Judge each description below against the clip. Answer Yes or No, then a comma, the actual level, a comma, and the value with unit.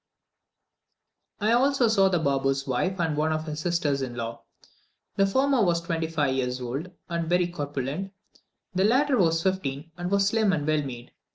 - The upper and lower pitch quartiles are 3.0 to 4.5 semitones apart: No, wide, 5.6 semitones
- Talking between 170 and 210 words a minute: Yes, average, 175 wpm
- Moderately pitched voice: Yes, medium, 165 Hz